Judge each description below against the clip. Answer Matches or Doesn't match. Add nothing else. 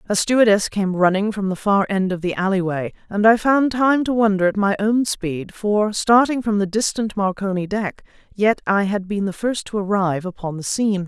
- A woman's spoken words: Matches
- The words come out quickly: Matches